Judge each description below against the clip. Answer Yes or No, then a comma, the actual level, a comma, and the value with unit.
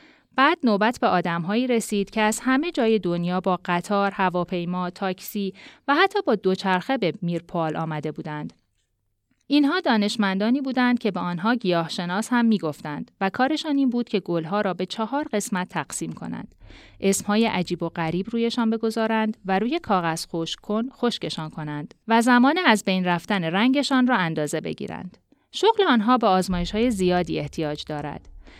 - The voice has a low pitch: No, high, 200 Hz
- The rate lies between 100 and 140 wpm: No, fast, 155 wpm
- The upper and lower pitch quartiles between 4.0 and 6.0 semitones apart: Yes, wide, 5.4 semitones